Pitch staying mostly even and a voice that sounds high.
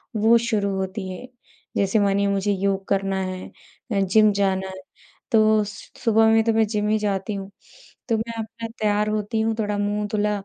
Yes: narrow, 1.8 semitones; high, 210 Hz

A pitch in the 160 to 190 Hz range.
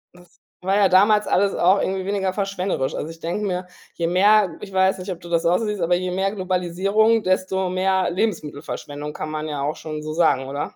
Yes: medium, 185 Hz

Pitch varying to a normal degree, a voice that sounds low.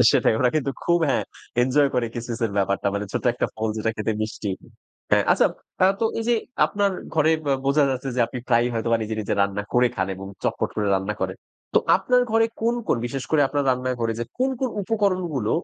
No: wide, 6.5 semitones; low, 125 Hz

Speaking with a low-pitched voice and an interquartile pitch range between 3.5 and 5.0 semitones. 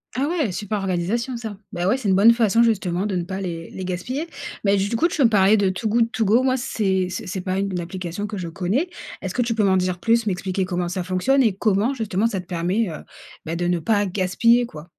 No: high, 195 Hz; average, 4.0 semitones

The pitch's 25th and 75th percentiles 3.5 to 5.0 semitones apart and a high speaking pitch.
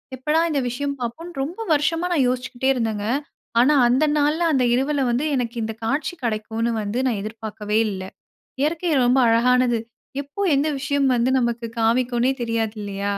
Yes: average, 3.8 semitones; very high, 250 Hz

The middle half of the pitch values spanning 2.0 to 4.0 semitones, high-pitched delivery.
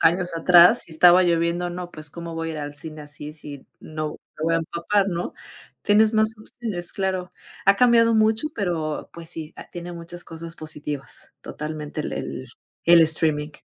No: narrow, 2.6 semitones; medium, 170 Hz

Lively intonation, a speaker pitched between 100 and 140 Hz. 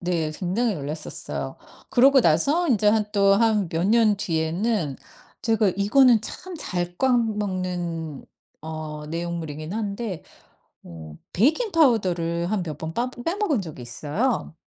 No: wide, 6.1 semitones; high, 190 Hz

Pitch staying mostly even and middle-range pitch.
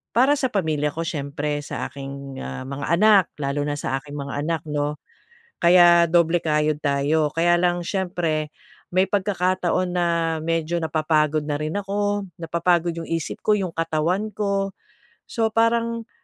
No: average, 4.0 semitones; medium, 165 Hz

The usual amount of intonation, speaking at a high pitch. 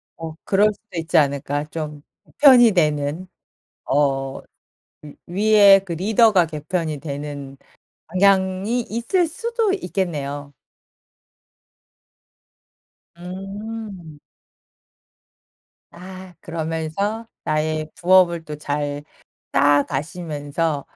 No: average, 5.0 semitones; medium, 165 Hz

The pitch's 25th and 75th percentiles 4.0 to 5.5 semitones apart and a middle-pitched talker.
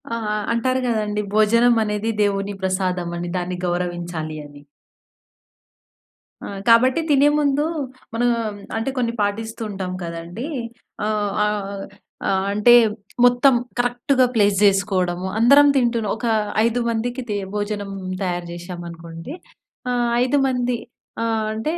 No: average, 4.6 semitones; high, 210 Hz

